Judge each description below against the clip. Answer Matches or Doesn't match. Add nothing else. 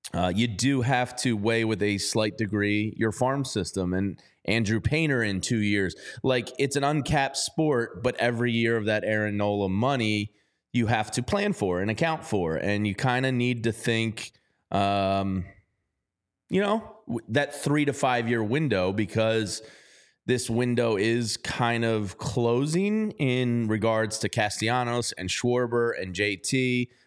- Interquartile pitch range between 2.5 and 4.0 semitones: Matches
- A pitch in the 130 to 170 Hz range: Doesn't match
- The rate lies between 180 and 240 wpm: Doesn't match